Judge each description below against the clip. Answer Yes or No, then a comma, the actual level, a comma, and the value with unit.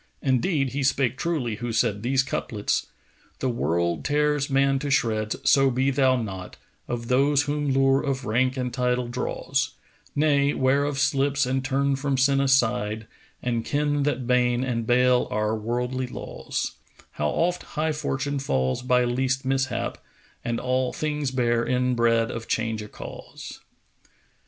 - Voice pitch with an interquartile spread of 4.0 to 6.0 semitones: No, narrow, 2.5 semitones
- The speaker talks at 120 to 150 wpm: No, average, 160 wpm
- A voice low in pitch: Yes, low, 130 Hz